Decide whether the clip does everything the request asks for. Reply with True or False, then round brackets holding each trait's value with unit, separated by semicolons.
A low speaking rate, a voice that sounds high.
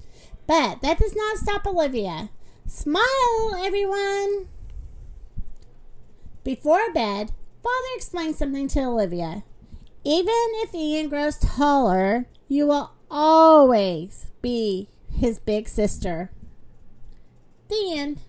True (95 wpm; 295 Hz)